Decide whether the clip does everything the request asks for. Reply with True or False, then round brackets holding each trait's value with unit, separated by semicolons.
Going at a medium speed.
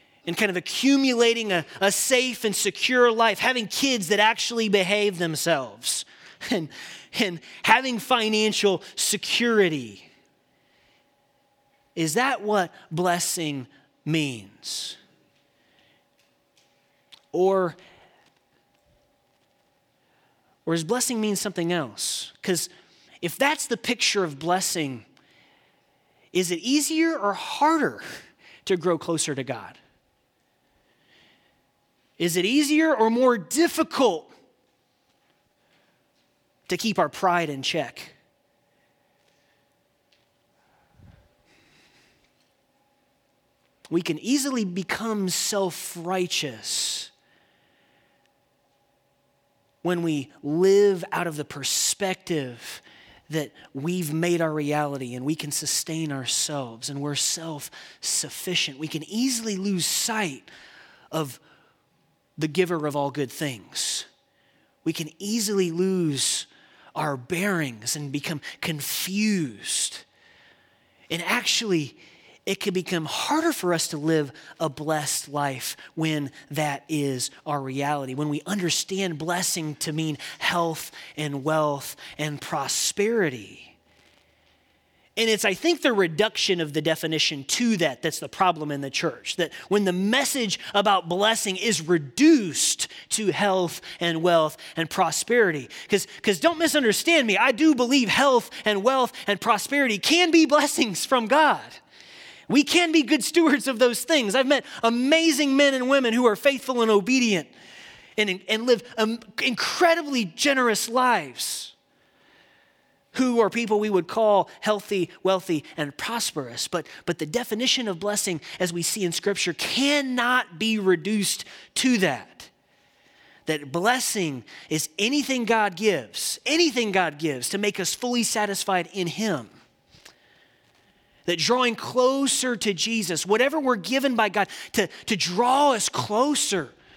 False (120 wpm)